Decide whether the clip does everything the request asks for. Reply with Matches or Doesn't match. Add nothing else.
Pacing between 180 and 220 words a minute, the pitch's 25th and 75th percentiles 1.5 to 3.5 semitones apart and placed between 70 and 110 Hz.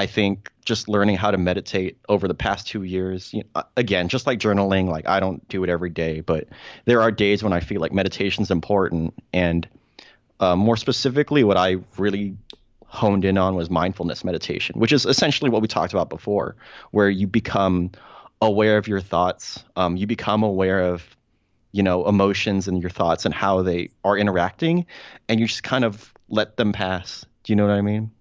Matches